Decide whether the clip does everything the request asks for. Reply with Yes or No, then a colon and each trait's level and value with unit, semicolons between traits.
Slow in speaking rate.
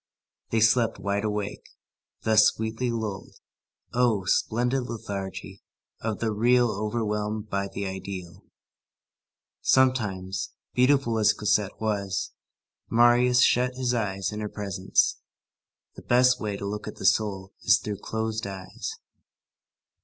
Yes: slow, 125 wpm